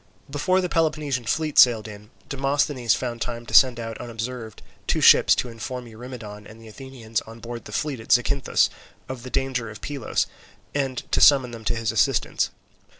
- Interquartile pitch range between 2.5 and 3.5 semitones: Yes, average, 3.0 semitones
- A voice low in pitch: Yes, low, 120 Hz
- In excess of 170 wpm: Yes, average, 180 wpm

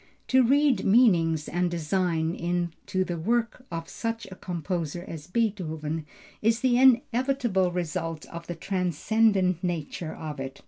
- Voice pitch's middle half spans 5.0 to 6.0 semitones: Yes, wide, 5.6 semitones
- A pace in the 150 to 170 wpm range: No, slow, 135 wpm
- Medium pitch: Yes, medium, 180 Hz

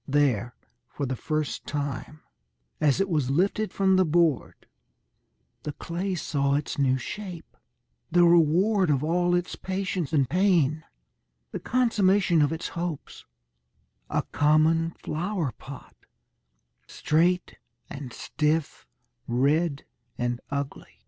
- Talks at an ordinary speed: No, slow, 115 wpm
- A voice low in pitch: No, medium, 160 Hz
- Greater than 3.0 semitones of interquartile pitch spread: Yes, average, 3.9 semitones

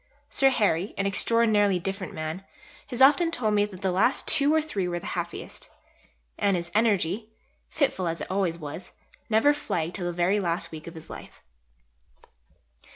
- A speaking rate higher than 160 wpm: Yes, average, 170 wpm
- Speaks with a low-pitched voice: No, high, 195 Hz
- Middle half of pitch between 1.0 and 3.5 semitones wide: No, average, 4.6 semitones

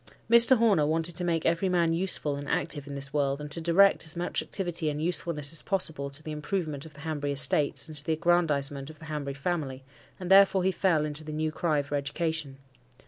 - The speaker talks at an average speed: No, fast, 215 wpm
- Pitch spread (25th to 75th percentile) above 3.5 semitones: No, average, 3.1 semitones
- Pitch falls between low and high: Yes, medium, 155 Hz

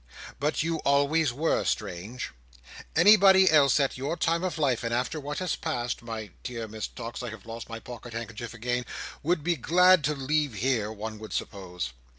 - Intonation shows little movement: No, wide, 5.6 semitones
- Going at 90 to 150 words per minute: No, average, 170 wpm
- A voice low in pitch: Yes, low, 125 Hz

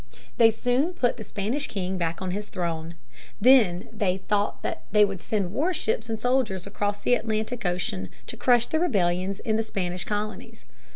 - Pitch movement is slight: No, average, 4.3 semitones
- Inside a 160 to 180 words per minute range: Yes, average, 175 wpm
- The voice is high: Yes, high, 210 Hz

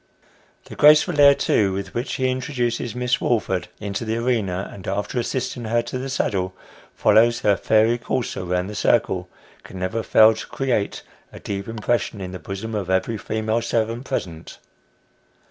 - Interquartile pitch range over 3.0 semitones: Yes, average, 3.6 semitones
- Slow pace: No, average, 165 wpm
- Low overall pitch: Yes, low, 110 Hz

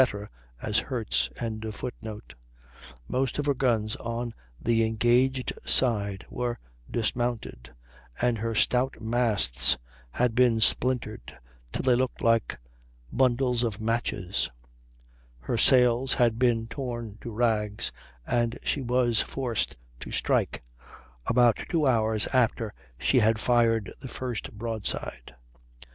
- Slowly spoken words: Yes, slow, 115 wpm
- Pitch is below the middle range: Yes, low, 120 Hz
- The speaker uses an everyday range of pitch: No, narrow, 2.1 semitones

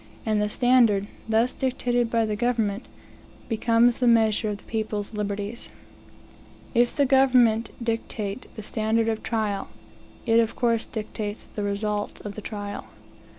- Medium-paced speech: Yes, average, 145 wpm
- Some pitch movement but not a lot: No, narrow, 2.2 semitones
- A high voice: Yes, high, 220 Hz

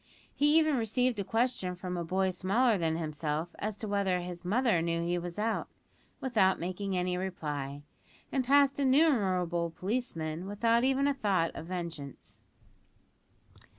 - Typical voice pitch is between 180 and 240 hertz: Yes, high, 190 Hz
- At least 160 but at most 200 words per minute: No, average, 150 wpm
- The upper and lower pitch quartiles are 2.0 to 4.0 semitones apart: No, wide, 5.6 semitones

